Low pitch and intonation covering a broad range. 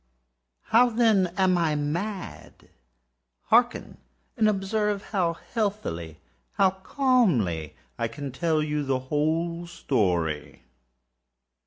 No: medium, 165 Hz; wide, 7.7 semitones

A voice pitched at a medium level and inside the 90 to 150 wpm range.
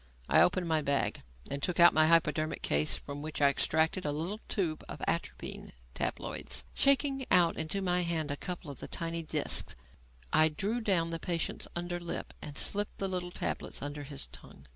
No: medium, 165 Hz; average, 185 wpm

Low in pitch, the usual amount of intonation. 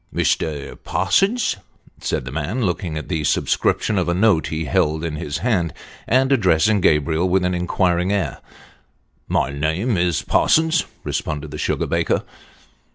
Yes: very low, 85 Hz; average, 4.6 semitones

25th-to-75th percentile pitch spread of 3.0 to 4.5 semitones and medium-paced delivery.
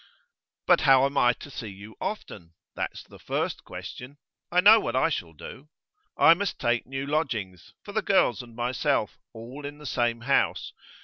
Yes: average, 4.1 semitones; average, 180 wpm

